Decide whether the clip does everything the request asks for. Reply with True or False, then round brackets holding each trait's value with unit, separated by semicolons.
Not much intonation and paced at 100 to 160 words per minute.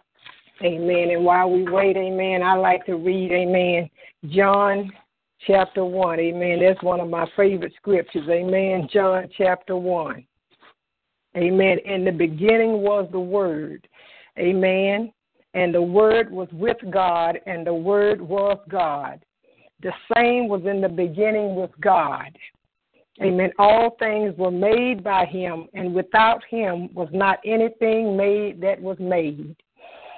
True (2.2 semitones; 135 wpm)